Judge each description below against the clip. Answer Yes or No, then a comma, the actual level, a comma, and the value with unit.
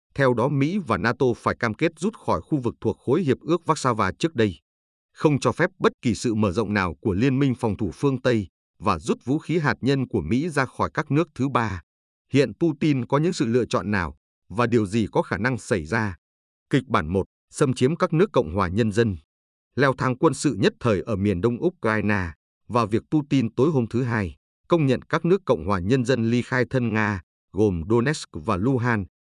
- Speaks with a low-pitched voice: Yes, low, 120 Hz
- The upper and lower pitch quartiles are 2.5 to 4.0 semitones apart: No, average, 5.2 semitones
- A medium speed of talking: Yes, average, 225 wpm